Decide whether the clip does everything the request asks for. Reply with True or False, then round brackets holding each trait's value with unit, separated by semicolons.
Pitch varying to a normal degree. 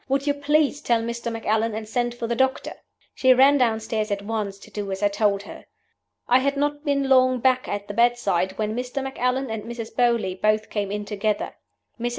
True (3.6 semitones)